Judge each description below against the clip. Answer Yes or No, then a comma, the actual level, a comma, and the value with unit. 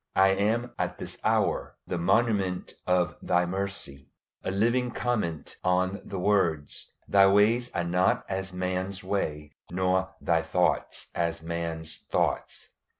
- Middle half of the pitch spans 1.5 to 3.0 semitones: Yes, narrow, 2.6 semitones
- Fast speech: No, slow, 135 wpm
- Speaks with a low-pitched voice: Yes, very low, 95 Hz